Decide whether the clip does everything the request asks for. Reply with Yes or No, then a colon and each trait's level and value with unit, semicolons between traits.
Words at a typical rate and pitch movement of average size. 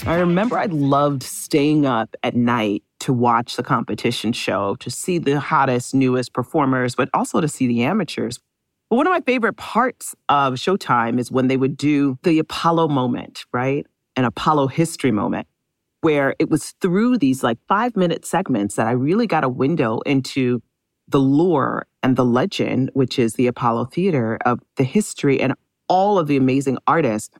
Yes: average, 175 wpm; average, 4.3 semitones